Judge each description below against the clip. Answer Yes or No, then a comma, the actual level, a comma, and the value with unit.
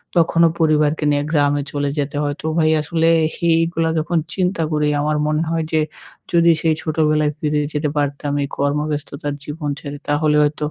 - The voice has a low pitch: No, medium, 150 Hz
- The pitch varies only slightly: Yes, narrow, 1.8 semitones